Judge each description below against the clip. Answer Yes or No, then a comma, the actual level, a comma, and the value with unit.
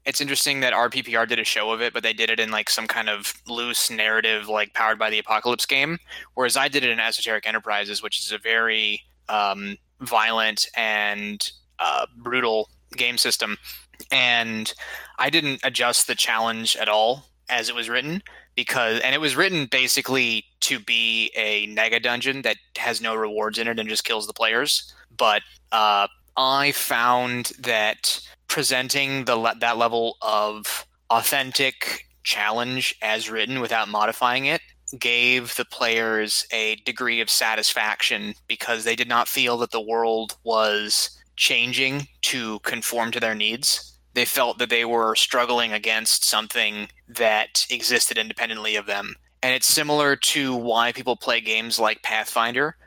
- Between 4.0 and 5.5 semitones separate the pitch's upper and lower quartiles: No, narrow, 2.6 semitones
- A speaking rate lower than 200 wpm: Yes, average, 160 wpm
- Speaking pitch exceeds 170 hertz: No, low, 115 Hz